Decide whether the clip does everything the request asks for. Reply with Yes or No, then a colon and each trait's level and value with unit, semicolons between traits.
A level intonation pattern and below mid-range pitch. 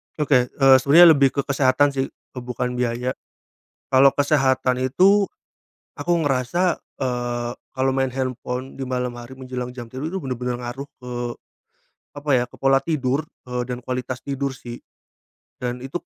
Yes: narrow, 1.8 semitones; low, 130 Hz